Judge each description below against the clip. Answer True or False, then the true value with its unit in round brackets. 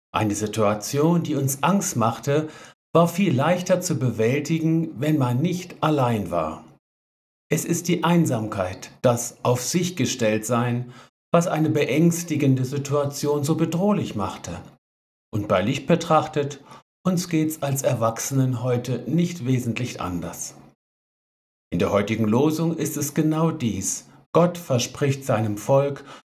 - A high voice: False (140 Hz)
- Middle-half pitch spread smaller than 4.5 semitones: False (5.4 semitones)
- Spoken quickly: False (130 wpm)